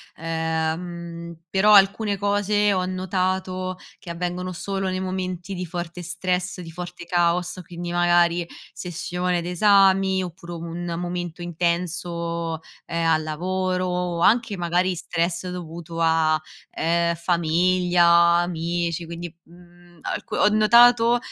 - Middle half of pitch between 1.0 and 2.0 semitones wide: Yes, narrow, 1.6 semitones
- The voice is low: No, medium, 175 Hz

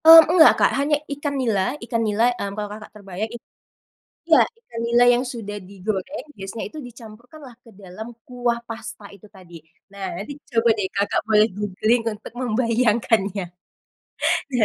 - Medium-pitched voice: No, high, 225 Hz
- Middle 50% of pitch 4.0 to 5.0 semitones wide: No, average, 3.0 semitones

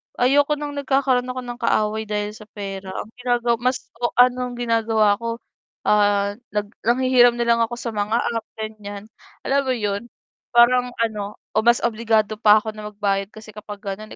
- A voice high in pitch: Yes, high, 225 Hz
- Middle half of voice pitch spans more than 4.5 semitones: No, average, 2.7 semitones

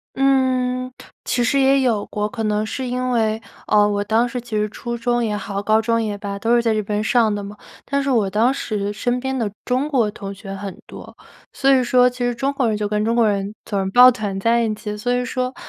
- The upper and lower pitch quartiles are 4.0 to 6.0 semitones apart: No, average, 3.1 semitones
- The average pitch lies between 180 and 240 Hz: Yes, high, 230 Hz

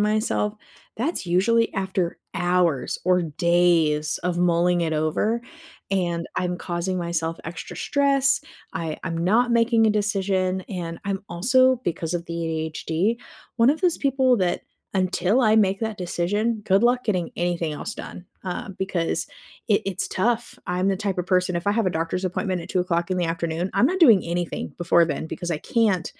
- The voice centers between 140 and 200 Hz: Yes, medium, 185 Hz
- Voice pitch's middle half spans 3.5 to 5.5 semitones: Yes, average, 3.8 semitones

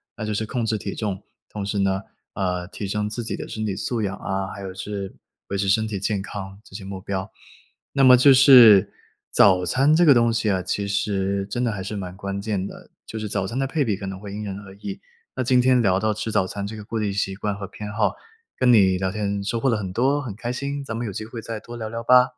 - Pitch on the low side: Yes, low, 105 Hz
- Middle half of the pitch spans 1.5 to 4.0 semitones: Yes, average, 2.9 semitones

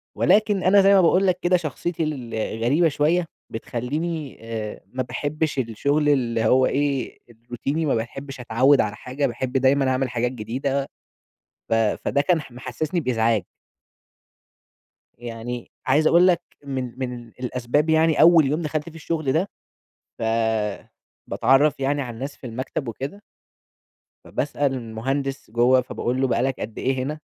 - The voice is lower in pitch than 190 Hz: Yes, low, 135 Hz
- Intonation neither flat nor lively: Yes, average, 4.0 semitones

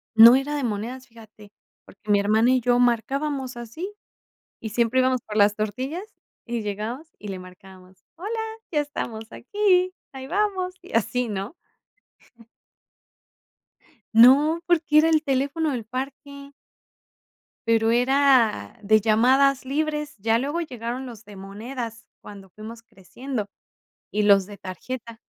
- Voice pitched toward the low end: No, high, 240 Hz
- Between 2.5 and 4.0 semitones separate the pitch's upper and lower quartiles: No, average, 4.6 semitones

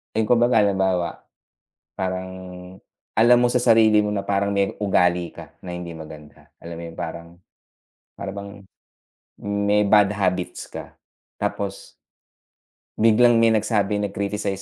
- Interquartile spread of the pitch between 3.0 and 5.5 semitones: No, narrow, 2.5 semitones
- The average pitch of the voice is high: No, low, 100 Hz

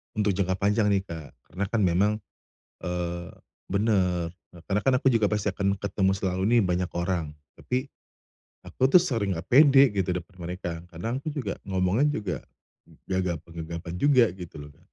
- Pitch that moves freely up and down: No, average, 3.5 semitones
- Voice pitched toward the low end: Yes, very low, 95 Hz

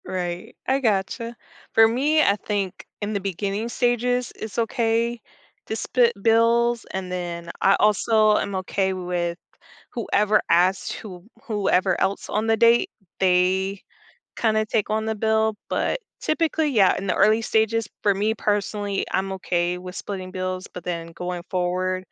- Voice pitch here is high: Yes, high, 205 Hz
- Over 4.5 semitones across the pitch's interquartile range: No, average, 3.4 semitones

